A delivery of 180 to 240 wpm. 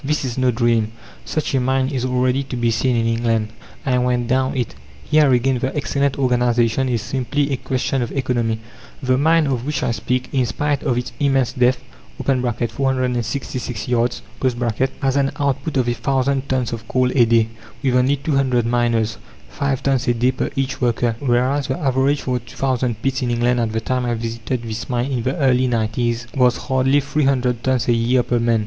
Yes: average, 200 wpm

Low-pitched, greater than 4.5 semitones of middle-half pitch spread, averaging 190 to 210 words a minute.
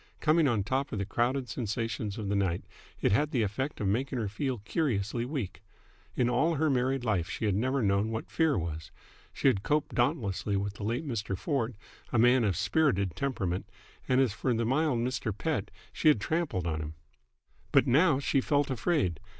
Yes: low, 120 Hz; wide, 5.4 semitones; average, 200 wpm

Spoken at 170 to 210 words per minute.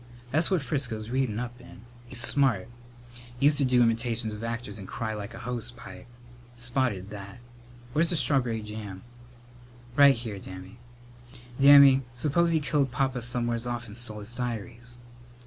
No: average, 155 wpm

